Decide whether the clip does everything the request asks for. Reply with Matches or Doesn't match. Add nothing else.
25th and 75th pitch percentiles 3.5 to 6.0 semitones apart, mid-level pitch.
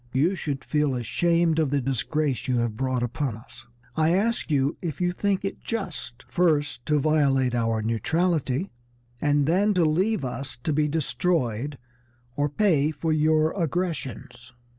Matches